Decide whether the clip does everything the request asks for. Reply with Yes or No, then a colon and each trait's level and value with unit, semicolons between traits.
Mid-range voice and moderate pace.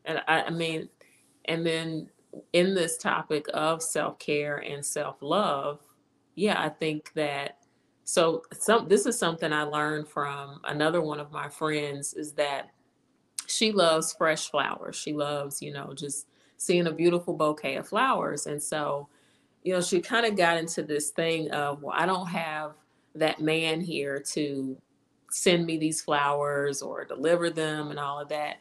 Yes: medium, 155 Hz; average, 165 wpm